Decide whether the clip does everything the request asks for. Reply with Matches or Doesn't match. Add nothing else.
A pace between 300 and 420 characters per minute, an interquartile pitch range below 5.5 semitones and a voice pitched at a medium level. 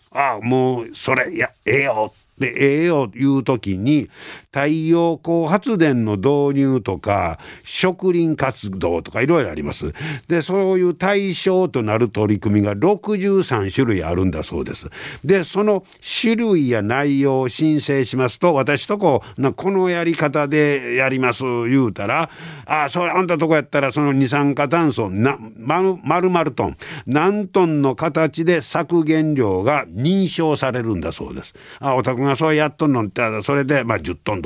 Matches